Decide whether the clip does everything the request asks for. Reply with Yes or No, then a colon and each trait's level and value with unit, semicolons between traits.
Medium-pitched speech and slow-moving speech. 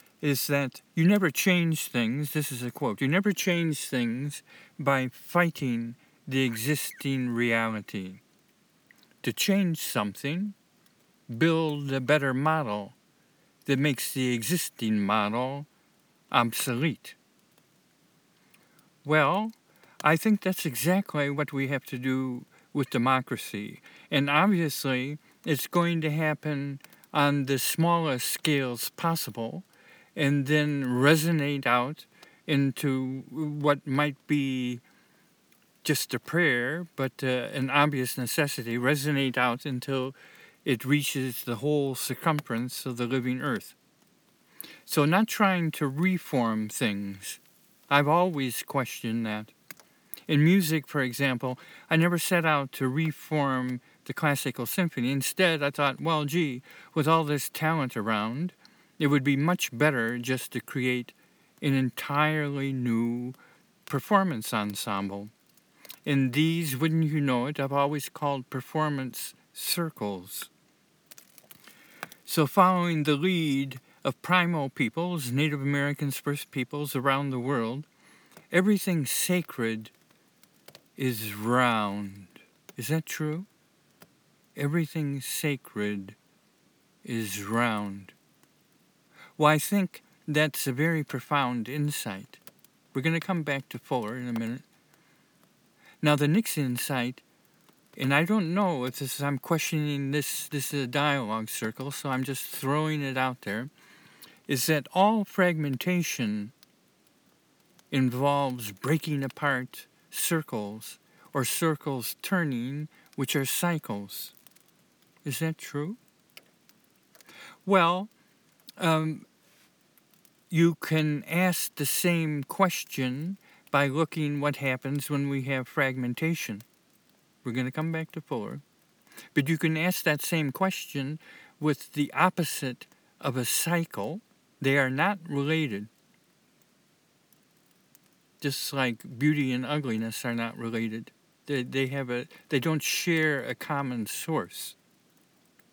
Yes: medium, 145 Hz; slow, 115 wpm